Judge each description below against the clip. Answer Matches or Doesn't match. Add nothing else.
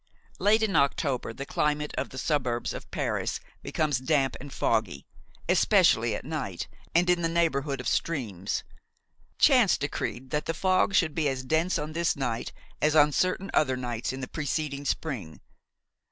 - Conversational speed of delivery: Matches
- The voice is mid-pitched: Matches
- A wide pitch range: Doesn't match